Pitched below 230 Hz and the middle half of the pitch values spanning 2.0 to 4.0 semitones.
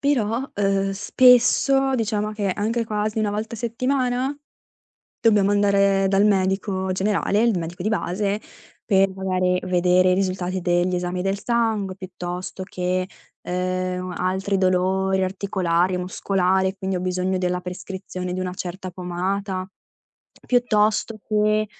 Yes: high, 190 Hz; narrow, 2.4 semitones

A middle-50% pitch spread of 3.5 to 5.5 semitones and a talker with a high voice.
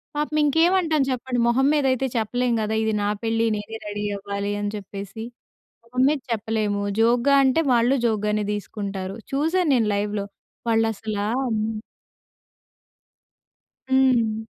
Yes: average, 4.1 semitones; high, 225 Hz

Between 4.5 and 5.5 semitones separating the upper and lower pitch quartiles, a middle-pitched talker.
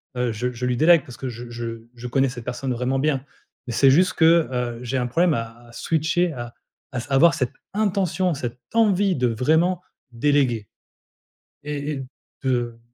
No: average, 5.1 semitones; low, 130 Hz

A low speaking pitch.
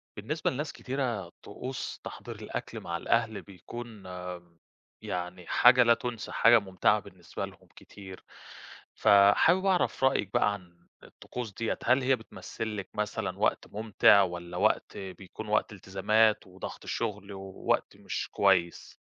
Yes: low, 105 Hz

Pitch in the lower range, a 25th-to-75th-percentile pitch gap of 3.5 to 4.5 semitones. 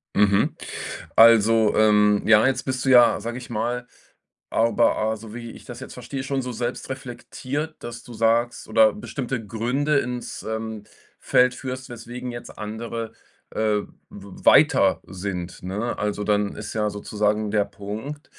No: low, 115 Hz; average, 2.8 semitones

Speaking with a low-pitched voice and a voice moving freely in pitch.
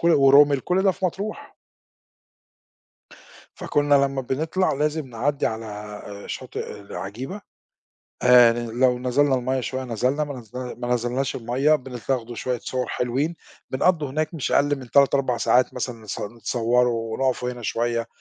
No: low, 130 Hz; average, 3.2 semitones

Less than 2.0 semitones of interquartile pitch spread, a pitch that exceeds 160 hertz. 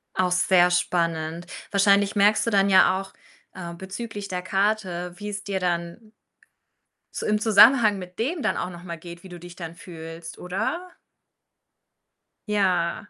No: average, 2.9 semitones; medium, 185 Hz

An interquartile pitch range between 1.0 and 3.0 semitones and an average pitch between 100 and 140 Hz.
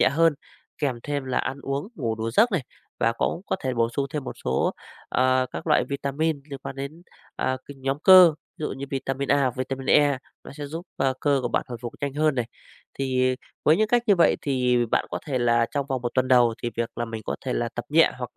Yes: average, 2.7 semitones; low, 135 Hz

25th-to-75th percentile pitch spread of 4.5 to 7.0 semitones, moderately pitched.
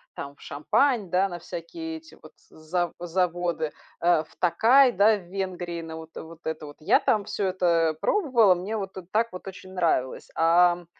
No: average, 3.4 semitones; medium, 180 Hz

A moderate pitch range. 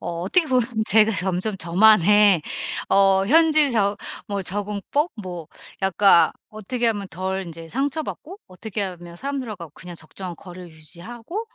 Yes: average, 4.3 semitones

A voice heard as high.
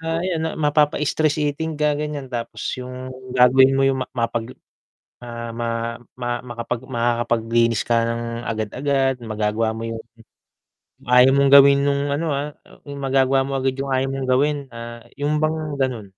No: low, 130 Hz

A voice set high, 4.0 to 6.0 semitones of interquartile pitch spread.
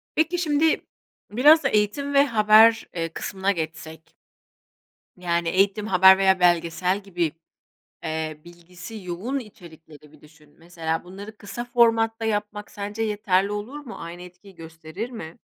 Yes: high, 195 Hz; average, 4.8 semitones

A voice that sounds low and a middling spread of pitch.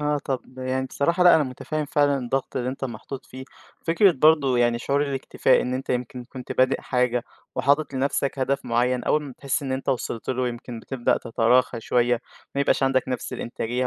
No: low, 130 Hz; narrow, 2.1 semitones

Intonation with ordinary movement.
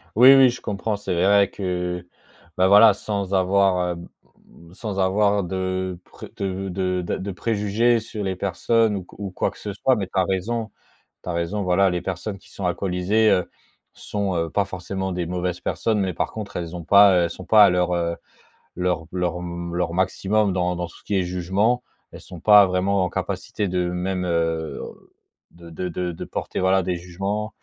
No: narrow, 2.3 semitones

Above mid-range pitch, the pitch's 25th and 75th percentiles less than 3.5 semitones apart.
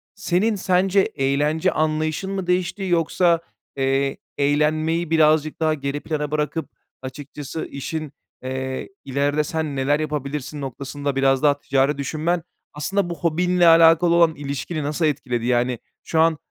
No: medium, 150 Hz; average, 3.0 semitones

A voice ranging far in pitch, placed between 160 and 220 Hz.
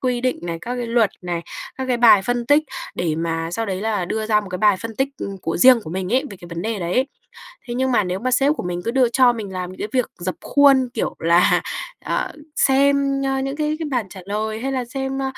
No: wide, 5.9 semitones; high, 230 Hz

